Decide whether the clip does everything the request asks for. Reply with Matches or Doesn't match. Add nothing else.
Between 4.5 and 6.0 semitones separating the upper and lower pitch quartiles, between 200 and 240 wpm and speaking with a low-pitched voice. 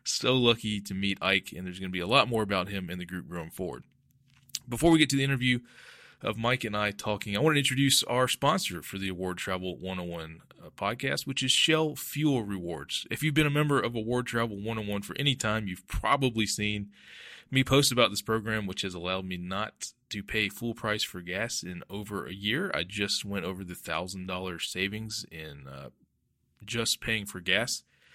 Matches